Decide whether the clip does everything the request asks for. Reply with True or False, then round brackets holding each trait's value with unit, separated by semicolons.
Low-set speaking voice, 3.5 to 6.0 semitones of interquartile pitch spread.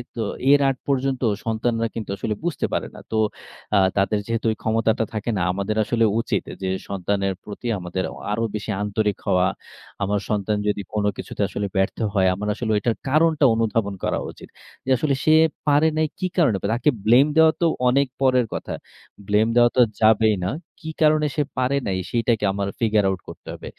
True (110 Hz; 3.9 semitones)